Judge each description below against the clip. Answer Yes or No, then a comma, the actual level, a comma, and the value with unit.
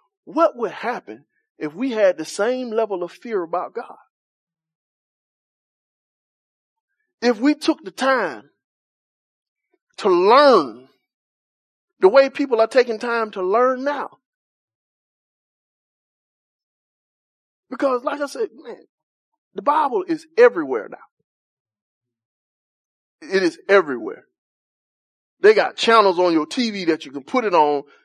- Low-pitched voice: No, very high, 250 Hz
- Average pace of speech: No, slow, 115 wpm